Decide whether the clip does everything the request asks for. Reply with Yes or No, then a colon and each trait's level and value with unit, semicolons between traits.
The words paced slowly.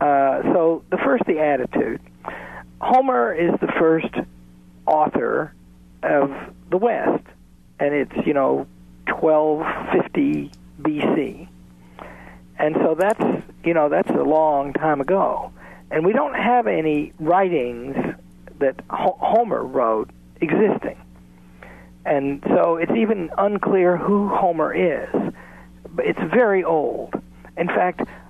Yes: slow, 125 wpm